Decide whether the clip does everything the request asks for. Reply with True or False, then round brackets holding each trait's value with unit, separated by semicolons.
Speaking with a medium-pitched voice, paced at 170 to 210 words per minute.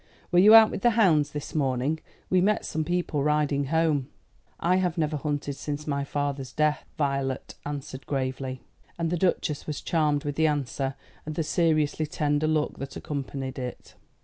True (150 Hz; 175 wpm)